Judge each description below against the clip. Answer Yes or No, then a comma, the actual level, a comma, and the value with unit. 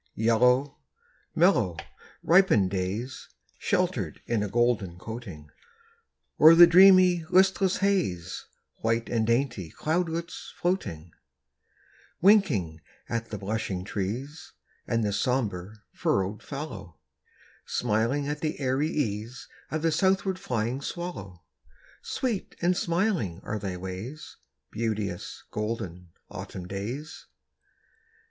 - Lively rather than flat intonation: Yes, wide, 8.5 semitones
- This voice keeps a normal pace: No, slow, 105 wpm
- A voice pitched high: No, low, 115 Hz